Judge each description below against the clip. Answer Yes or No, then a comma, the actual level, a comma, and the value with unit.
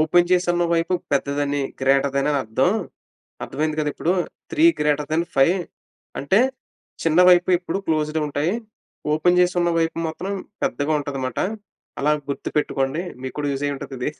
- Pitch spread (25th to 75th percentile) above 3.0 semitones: Yes, average, 3.5 semitones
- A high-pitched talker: No, medium, 150 Hz